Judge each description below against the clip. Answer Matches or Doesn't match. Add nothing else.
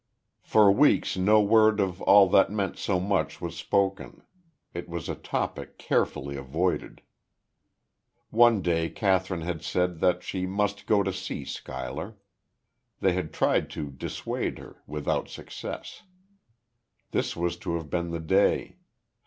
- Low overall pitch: Matches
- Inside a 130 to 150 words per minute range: Matches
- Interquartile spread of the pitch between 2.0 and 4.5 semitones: Matches